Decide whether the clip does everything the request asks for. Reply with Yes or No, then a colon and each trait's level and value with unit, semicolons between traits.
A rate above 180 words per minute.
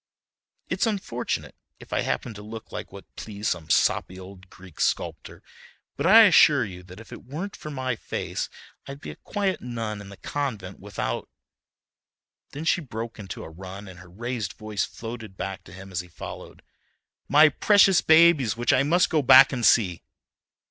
No: average, 175 wpm